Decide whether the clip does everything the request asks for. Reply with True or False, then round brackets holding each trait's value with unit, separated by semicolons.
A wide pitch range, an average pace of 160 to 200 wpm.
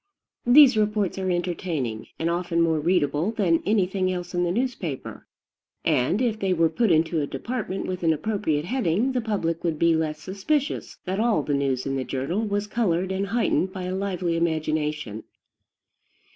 False (4.3 semitones; 170 wpm)